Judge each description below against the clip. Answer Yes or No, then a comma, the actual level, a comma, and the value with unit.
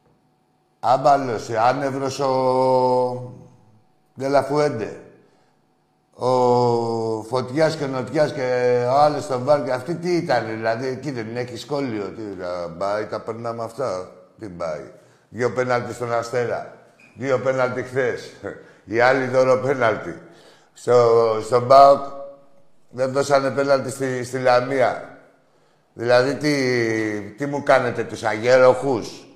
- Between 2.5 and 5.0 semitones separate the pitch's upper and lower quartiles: Yes, average, 2.9 semitones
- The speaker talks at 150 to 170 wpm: No, slow, 115 wpm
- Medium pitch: No, low, 125 Hz